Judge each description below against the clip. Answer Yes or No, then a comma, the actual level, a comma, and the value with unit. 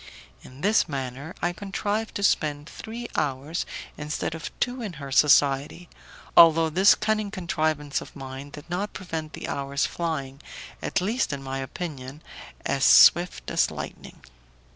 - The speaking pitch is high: No, medium, 155 Hz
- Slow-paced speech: No, average, 145 wpm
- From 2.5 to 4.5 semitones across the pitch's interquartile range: No, average, 4.9 semitones